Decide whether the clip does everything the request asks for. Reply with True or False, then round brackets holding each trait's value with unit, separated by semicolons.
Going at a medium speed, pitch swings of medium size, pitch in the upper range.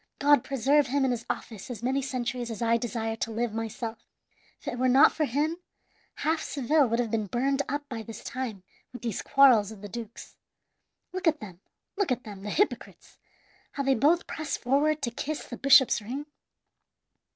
True (190 wpm; 3.8 semitones; 250 Hz)